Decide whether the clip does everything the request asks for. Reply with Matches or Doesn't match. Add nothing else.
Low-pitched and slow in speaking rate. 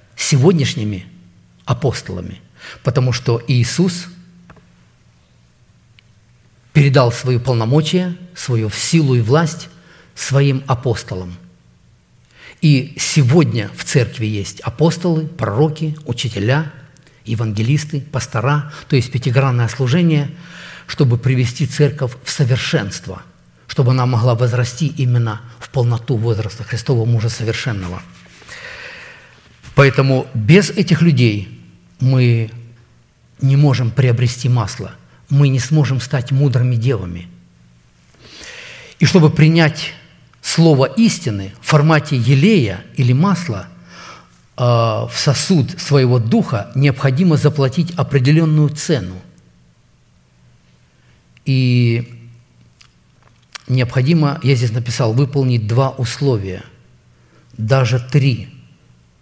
Matches